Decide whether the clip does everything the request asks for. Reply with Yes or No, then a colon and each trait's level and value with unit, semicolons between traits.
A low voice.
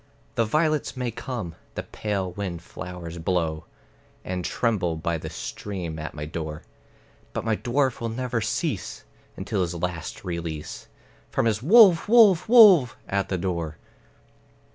Yes: very low, 95 Hz